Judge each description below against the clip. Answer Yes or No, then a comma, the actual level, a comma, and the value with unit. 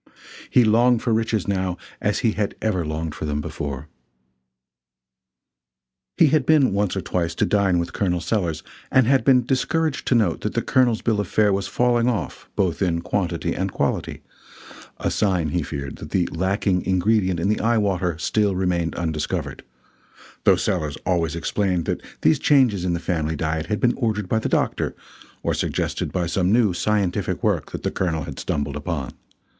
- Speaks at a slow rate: No, average, 180 wpm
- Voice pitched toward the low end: Yes, very low, 95 Hz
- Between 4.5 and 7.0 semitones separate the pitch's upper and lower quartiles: Yes, average, 4.8 semitones